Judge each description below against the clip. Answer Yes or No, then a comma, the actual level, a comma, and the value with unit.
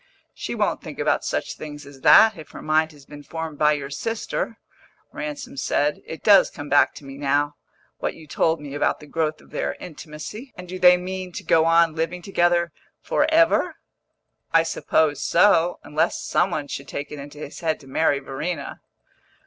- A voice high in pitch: No, medium, 160 Hz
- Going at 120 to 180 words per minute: No, average, 190 wpm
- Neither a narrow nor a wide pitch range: Yes, average, 3.5 semitones